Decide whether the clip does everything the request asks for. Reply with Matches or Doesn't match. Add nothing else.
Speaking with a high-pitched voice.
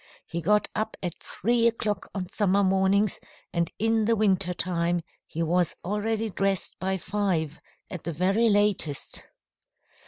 Matches